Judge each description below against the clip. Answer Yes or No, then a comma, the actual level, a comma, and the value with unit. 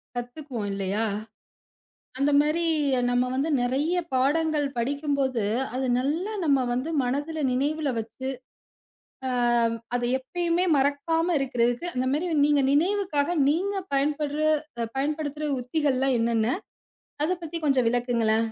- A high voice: Yes, very high, 280 Hz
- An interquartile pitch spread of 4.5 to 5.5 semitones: No, average, 3.9 semitones